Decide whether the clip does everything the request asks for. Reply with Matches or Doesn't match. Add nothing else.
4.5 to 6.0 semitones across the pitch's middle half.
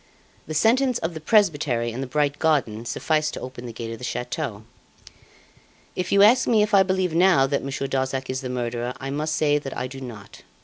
Matches